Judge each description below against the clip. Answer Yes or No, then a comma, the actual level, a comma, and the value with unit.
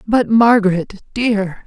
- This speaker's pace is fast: No, slow, 110 wpm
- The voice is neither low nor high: No, high, 210 Hz